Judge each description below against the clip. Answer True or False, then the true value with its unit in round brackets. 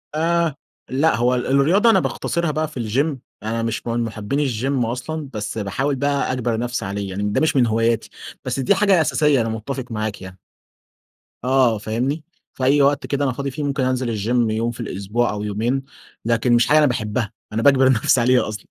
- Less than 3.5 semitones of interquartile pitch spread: False (3.9 semitones)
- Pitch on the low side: True (125 Hz)